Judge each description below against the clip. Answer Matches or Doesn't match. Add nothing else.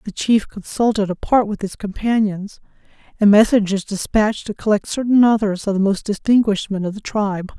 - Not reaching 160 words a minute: Doesn't match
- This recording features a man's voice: Doesn't match